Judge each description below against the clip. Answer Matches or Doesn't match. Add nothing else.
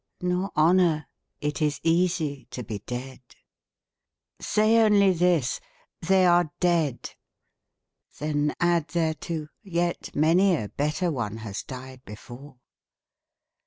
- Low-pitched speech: Doesn't match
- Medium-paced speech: Doesn't match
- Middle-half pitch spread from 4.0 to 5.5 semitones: Matches